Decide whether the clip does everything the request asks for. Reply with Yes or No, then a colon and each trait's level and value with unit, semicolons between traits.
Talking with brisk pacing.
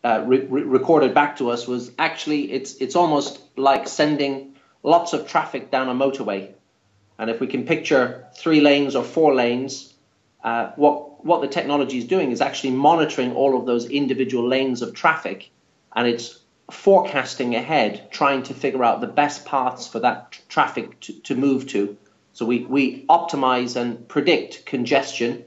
No: average, 170 wpm